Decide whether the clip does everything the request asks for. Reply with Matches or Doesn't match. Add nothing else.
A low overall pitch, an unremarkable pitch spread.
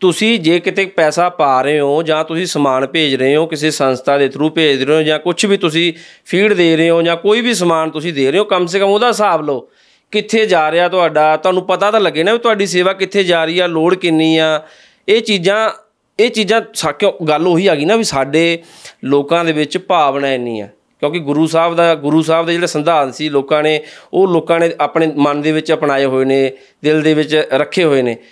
Doesn't match